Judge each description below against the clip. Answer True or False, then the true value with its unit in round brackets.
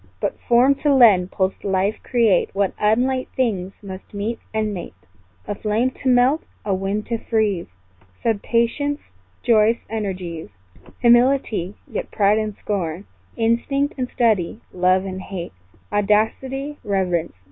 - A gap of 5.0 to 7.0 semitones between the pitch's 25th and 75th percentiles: False (3.9 semitones)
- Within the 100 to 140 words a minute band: True (135 wpm)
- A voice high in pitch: True (215 Hz)